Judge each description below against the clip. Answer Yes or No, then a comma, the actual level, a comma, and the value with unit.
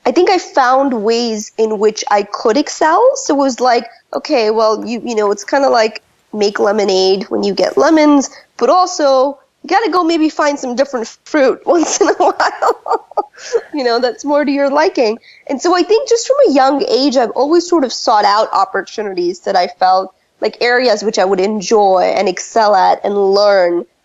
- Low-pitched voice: No, very high, 260 Hz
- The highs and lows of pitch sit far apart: Yes, wide, 7.0 semitones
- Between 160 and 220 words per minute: Yes, average, 200 wpm